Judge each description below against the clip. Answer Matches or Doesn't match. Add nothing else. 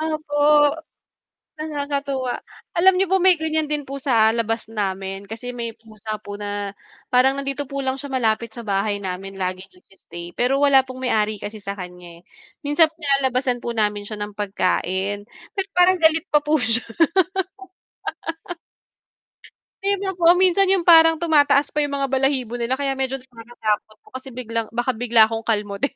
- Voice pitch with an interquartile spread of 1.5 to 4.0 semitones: Doesn't match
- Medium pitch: Doesn't match